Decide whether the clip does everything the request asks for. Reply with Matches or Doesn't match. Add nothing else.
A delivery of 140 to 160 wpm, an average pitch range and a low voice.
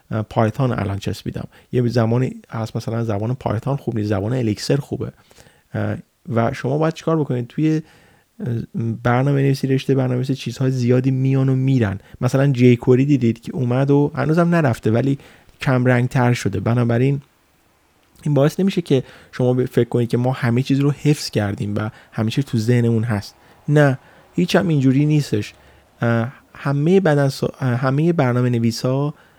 Matches